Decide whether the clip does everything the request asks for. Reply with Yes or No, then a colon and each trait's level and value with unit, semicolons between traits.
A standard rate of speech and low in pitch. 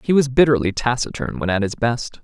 No: fast, 215 wpm; low, 125 Hz